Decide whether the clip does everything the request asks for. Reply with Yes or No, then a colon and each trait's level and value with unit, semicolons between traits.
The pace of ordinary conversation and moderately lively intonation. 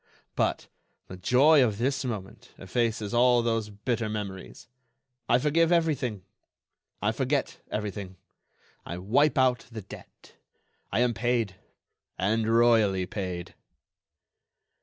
No: slow, 105 wpm; average, 3.8 semitones